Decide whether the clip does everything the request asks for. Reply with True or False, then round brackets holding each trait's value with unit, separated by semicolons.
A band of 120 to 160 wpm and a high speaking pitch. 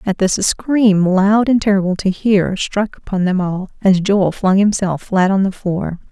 False (205 wpm; 195 Hz)